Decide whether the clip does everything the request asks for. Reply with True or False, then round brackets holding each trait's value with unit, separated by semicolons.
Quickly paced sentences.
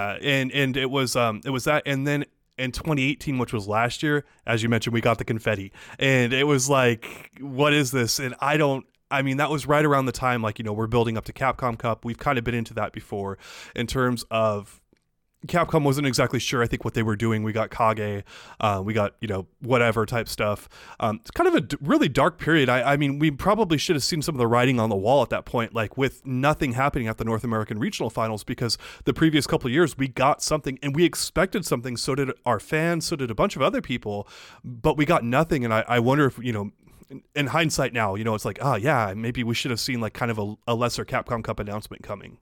True (255 wpm)